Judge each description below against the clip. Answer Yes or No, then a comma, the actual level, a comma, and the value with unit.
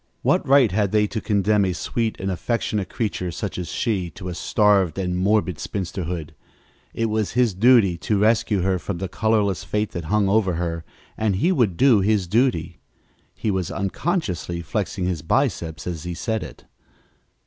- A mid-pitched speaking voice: No, low, 100 Hz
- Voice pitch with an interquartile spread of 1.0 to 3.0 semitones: No, average, 3.5 semitones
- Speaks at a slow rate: No, average, 175 wpm